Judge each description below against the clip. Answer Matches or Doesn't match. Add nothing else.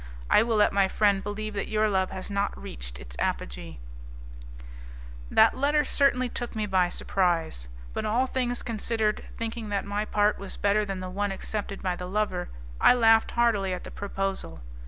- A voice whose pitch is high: Matches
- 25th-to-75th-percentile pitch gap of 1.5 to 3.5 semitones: Matches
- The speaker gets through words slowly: Doesn't match